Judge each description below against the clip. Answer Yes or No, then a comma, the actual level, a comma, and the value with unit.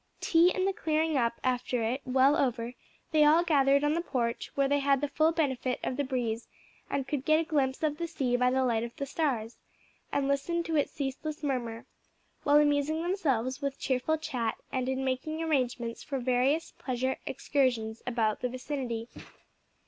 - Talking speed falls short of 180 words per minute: No, average, 185 wpm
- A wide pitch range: No, average, 3.4 semitones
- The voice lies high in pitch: Yes, very high, 270 Hz